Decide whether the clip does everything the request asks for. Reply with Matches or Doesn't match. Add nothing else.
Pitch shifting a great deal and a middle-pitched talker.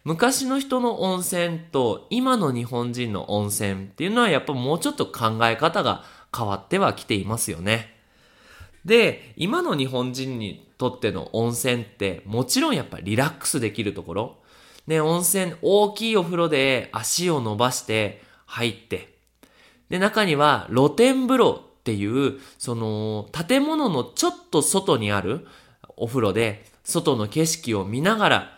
Doesn't match